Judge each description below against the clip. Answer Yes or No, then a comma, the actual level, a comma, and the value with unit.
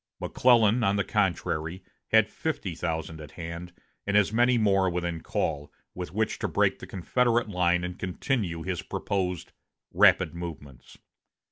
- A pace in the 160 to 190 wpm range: No, average, 145 wpm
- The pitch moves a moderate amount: Yes, average, 4.0 semitones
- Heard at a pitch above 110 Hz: No, very low, 90 Hz